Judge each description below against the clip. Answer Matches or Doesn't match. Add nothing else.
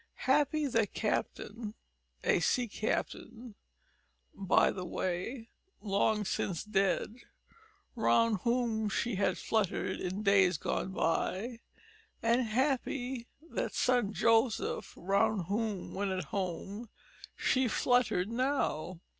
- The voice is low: Doesn't match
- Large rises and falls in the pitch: Doesn't match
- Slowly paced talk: Matches